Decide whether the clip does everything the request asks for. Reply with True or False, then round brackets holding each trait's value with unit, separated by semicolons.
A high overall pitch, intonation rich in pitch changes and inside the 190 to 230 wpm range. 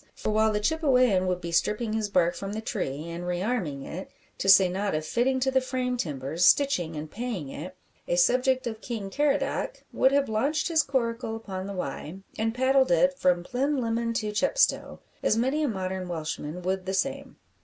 True (215 Hz; 6.2 semitones; 195 wpm)